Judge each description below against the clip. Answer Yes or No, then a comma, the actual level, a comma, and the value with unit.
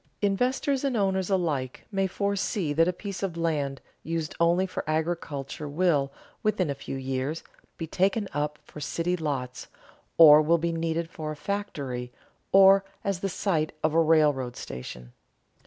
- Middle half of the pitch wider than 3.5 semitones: Yes, average, 4.5 semitones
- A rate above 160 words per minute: No, average, 155 wpm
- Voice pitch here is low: No, medium, 165 Hz